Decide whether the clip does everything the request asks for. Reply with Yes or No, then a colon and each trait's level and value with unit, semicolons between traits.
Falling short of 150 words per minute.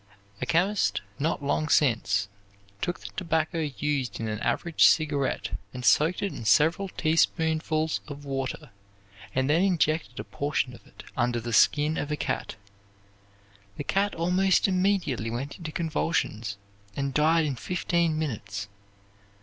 Yes: average, 140 wpm